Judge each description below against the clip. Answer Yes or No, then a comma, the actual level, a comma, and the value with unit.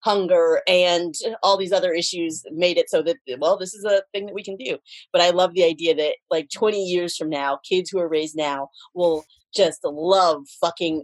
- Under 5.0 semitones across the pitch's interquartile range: Yes, average, 3.5 semitones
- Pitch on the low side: No, medium, 180 Hz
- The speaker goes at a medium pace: No, fast, 210 wpm